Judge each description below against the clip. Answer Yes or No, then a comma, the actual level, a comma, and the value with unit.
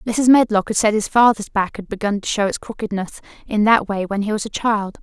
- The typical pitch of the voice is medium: No, high, 210 Hz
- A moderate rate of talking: No, fast, 250 wpm